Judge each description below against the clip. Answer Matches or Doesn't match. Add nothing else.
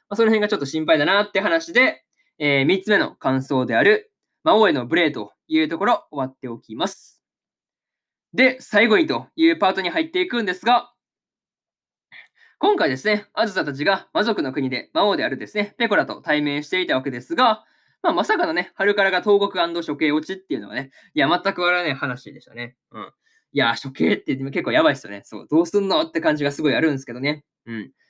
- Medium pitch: Matches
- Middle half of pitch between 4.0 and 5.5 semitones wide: Doesn't match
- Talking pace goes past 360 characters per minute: Matches